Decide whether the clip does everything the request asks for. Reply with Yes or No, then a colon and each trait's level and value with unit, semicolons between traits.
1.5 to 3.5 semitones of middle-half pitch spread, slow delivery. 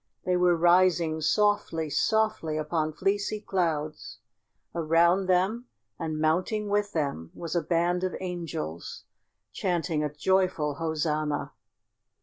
Yes: average, 3.2 semitones; slow, 115 wpm